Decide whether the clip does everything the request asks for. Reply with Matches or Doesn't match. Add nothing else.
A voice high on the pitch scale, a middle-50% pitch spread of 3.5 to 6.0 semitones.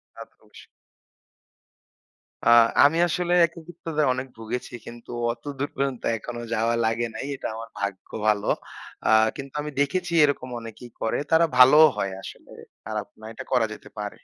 Doesn't match